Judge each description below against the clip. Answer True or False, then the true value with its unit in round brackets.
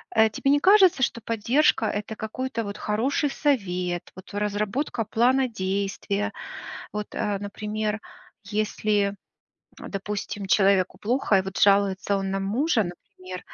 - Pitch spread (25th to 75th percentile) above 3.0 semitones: False (2.7 semitones)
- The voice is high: True (210 Hz)